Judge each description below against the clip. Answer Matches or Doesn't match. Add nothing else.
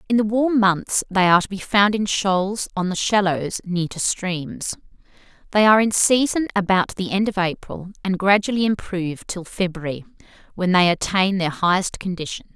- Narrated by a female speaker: Matches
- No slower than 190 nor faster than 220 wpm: Doesn't match